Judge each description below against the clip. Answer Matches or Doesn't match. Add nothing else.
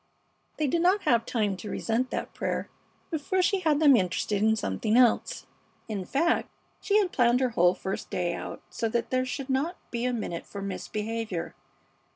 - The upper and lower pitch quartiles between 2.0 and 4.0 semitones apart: Doesn't match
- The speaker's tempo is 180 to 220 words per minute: Matches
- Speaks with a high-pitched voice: Matches